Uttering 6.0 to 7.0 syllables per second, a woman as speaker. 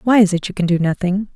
Yes: 6.6 syllables/s; female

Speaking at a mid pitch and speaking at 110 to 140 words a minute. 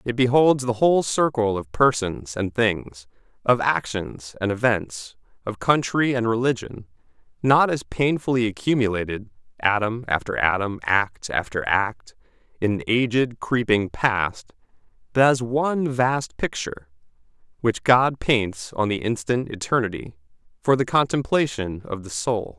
No: low, 115 Hz; slow, 135 wpm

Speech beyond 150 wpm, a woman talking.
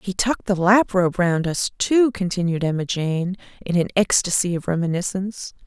Yes: average, 170 wpm; female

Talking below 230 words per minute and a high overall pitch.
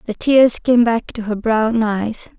Yes: average, 200 wpm; high, 225 Hz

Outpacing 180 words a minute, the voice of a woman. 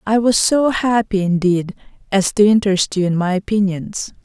No: average, 170 wpm; female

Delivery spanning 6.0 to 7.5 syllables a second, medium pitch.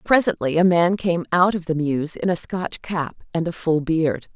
No: 4.5 syllables/s; medium, 170 Hz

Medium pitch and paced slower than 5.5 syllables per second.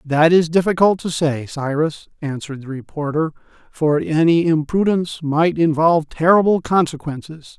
Yes: medium, 160 Hz; 4.9 syllables/s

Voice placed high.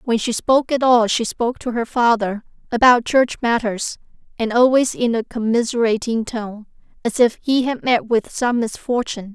Yes: high, 235 Hz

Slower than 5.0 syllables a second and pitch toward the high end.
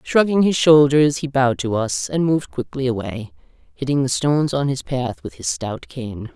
No: 4.8 syllables/s; low, 135 Hz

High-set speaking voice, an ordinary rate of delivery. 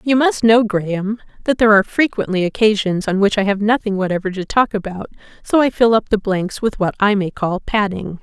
No: high, 210 Hz; fast, 220 wpm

